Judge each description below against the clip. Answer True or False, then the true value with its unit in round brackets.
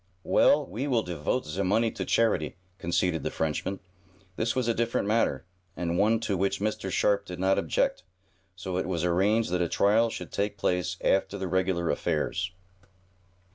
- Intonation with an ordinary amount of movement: True (3.4 semitones)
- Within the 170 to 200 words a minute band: True (175 wpm)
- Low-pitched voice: True (95 Hz)